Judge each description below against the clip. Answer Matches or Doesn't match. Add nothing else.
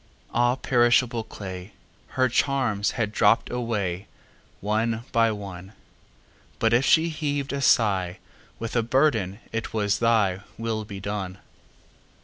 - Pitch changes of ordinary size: Matches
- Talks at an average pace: Doesn't match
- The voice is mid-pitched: Doesn't match